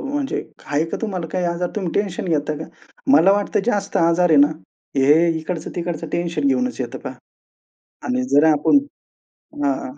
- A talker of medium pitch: Yes, medium, 170 Hz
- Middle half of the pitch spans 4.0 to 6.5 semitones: Yes, average, 4.3 semitones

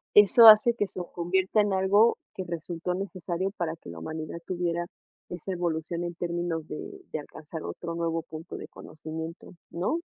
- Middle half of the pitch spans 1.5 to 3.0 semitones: Yes, narrow, 2.6 semitones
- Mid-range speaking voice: Yes, medium, 175 Hz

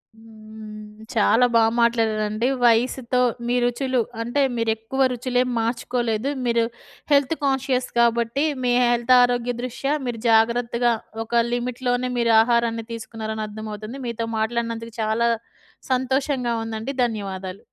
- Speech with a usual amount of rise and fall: No, narrow, 1.9 semitones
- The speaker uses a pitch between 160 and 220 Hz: No, high, 235 Hz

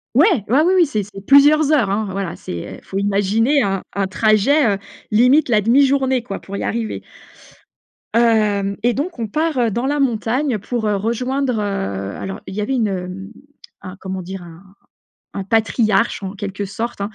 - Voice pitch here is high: Yes, high, 215 Hz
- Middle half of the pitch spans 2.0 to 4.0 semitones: No, average, 4.8 semitones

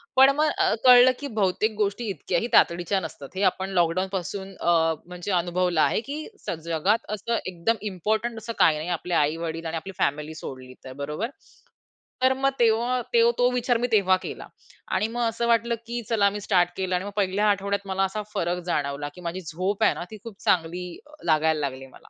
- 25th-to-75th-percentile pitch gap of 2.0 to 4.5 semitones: No, average, 5.1 semitones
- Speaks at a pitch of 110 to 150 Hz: No, high, 190 Hz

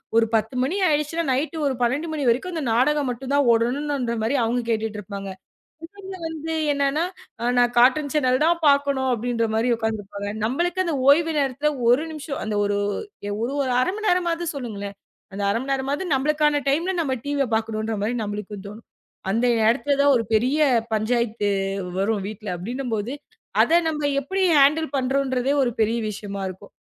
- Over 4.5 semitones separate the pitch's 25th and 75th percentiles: Yes, average, 4.9 semitones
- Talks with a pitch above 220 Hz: Yes, very high, 260 Hz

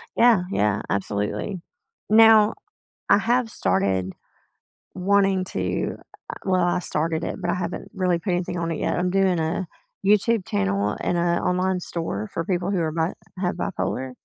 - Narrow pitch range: No, average, 3.5 semitones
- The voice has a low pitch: No, medium, 175 Hz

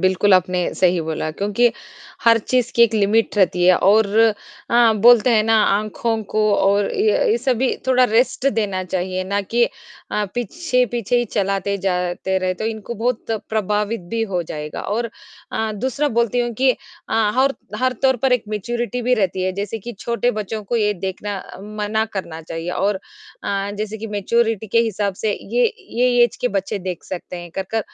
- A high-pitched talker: Yes, high, 215 Hz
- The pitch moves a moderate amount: Yes, average, 3.6 semitones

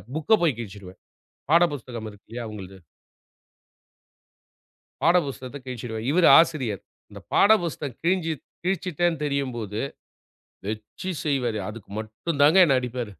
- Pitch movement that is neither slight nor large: No, wide, 6.8 semitones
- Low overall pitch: Yes, low, 130 Hz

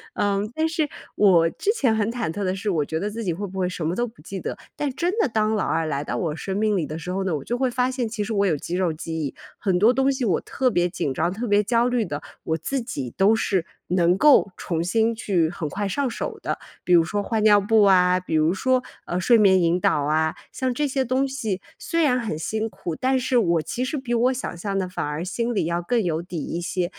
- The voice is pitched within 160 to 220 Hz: Yes, high, 200 Hz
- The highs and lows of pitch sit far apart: Yes, wide, 5.7 semitones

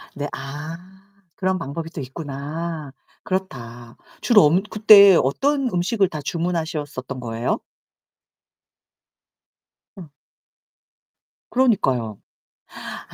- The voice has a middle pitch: Yes, medium, 160 Hz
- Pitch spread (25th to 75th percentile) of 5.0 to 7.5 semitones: Yes, wide, 5.6 semitones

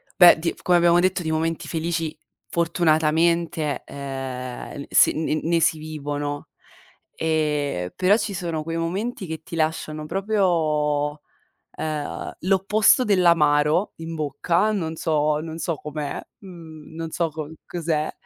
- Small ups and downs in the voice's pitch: Yes, narrow, 2.3 semitones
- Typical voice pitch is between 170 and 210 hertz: No, medium, 160 Hz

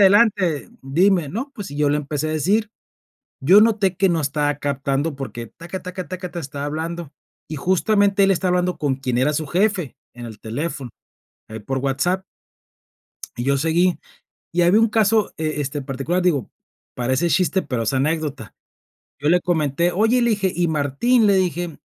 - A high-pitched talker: No, medium, 165 Hz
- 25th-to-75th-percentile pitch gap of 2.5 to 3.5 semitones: No, average, 5.2 semitones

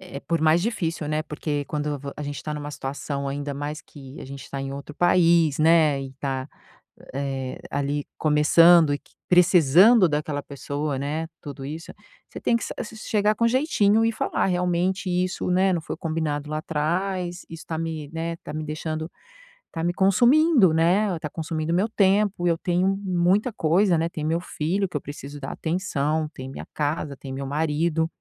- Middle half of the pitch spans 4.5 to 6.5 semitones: No, average, 3.6 semitones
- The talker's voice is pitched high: No, medium, 160 Hz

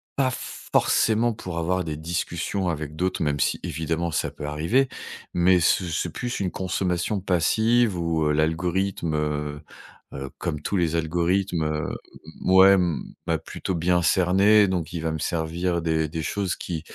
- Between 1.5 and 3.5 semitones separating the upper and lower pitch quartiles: Yes, average, 2.8 semitones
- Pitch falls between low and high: No, very low, 85 Hz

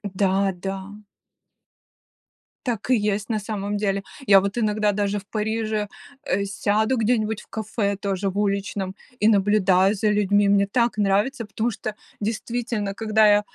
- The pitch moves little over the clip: Yes, narrow, 1.6 semitones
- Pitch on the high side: Yes, high, 205 Hz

